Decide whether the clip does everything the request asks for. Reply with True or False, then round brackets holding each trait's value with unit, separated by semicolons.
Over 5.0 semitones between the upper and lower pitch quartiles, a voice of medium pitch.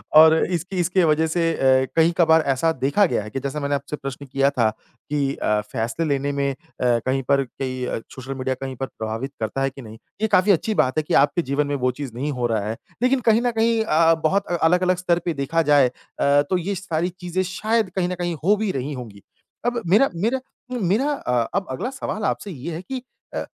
True (5.6 semitones; 155 Hz)